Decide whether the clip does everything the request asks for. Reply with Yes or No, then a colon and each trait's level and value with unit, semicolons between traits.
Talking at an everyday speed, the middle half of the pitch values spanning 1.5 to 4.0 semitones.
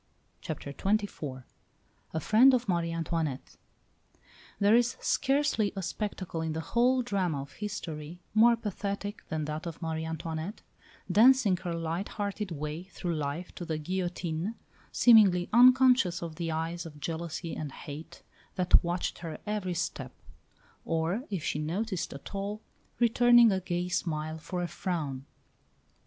No: average, 145 wpm; average, 4.6 semitones